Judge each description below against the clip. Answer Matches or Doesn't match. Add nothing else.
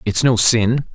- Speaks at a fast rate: Doesn't match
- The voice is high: Doesn't match